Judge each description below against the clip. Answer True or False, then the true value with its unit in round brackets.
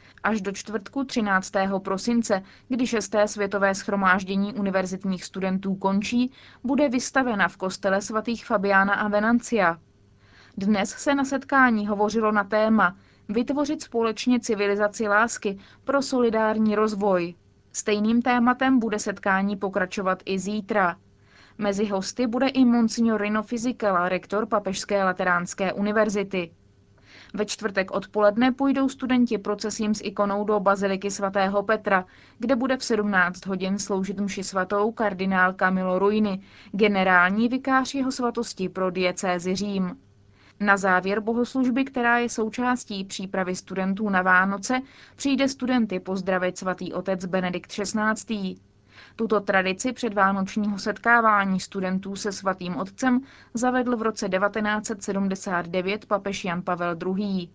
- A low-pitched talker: False (205 Hz)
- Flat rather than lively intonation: False (3.1 semitones)